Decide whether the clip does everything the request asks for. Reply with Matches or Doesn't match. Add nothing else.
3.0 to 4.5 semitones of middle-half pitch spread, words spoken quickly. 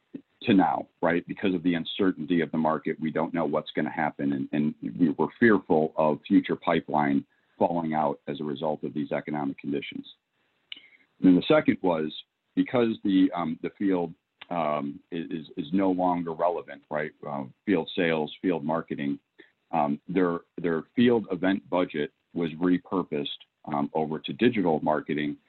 Doesn't match